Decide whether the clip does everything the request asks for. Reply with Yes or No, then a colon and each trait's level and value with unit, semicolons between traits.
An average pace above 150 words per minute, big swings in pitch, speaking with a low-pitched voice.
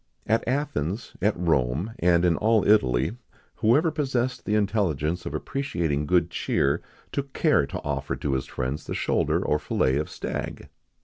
Yes: average, 160 wpm; wide, 7.7 semitones; very low, 90 Hz